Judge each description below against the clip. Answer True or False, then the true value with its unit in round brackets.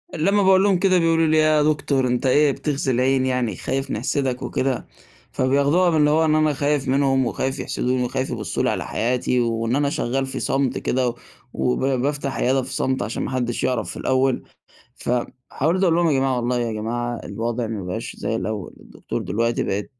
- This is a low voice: True (130 Hz)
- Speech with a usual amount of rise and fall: True (3.4 semitones)